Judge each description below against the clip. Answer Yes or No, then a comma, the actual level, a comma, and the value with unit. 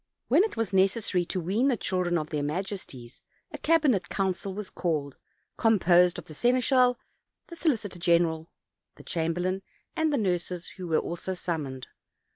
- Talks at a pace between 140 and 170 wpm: Yes, average, 155 wpm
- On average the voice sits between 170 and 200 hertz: Yes, medium, 185 Hz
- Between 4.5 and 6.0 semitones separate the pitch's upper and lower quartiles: Yes, average, 4.8 semitones